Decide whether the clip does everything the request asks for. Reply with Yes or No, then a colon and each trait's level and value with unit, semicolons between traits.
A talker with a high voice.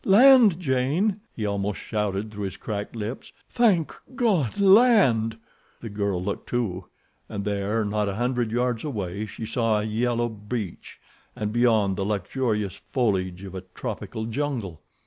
No: low, 110 Hz